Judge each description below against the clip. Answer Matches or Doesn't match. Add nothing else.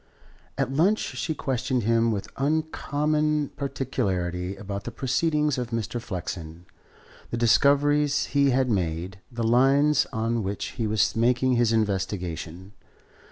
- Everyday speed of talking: Doesn't match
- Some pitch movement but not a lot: Doesn't match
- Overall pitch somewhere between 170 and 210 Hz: Doesn't match